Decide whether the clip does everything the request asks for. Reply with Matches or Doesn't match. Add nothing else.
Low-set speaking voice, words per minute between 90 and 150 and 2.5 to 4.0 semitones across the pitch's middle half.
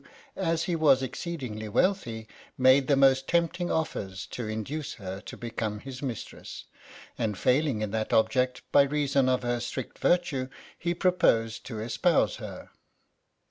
Doesn't match